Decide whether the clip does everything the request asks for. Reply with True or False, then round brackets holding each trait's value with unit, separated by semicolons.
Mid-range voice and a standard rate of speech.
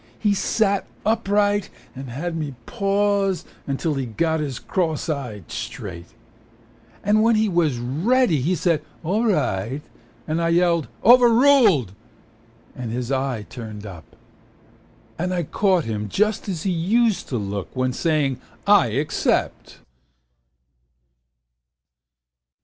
False (165 Hz; 120 wpm)